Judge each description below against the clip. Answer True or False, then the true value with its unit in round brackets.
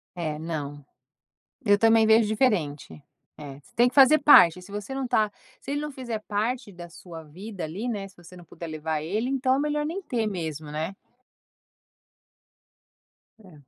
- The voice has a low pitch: False (205 Hz)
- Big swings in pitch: True (7.2 semitones)